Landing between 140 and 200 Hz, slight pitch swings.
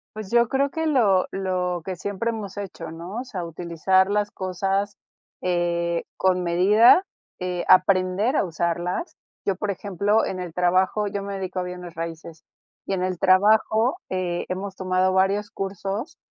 Yes: high, 190 Hz; narrow, 2.3 semitones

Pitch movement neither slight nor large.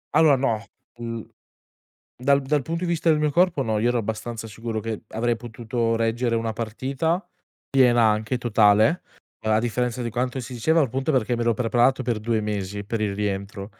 Yes: average, 3.2 semitones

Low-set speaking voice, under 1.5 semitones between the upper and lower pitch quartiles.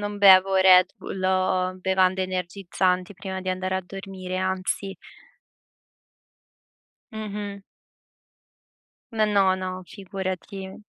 No: high, 190 Hz; narrow, 0.9 semitones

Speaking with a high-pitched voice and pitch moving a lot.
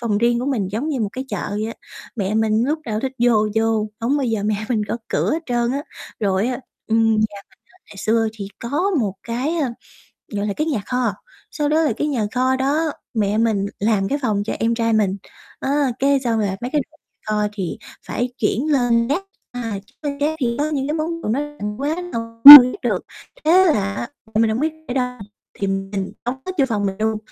No: high, 235 Hz; average, 4.6 semitones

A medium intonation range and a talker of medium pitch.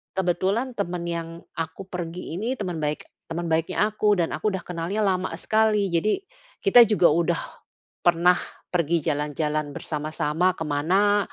Yes: average, 3.7 semitones; medium, 175 Hz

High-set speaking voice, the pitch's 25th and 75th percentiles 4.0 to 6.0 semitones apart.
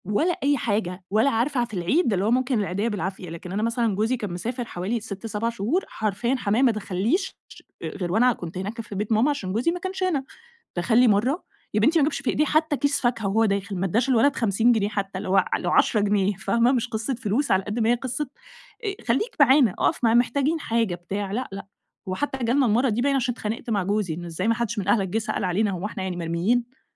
Yes: high, 225 Hz; average, 4.3 semitones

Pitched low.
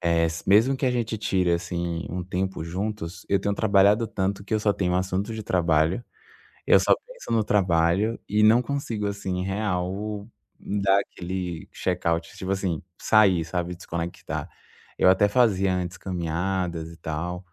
Yes: very low, 95 Hz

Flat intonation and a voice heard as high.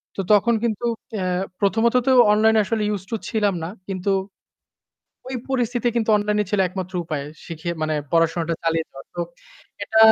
No: average, 4.5 semitones; high, 200 Hz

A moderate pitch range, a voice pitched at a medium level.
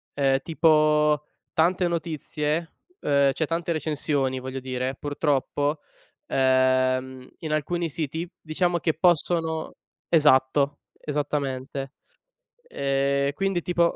Yes: average, 3.2 semitones; medium, 150 Hz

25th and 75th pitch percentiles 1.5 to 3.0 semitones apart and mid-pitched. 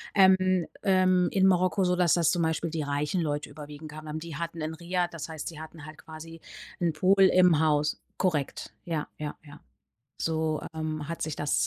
Yes: average, 2.7 semitones; medium, 160 Hz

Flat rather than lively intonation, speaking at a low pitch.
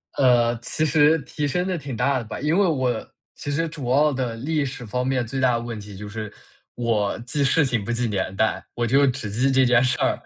No: average, 3.6 semitones; low, 125 Hz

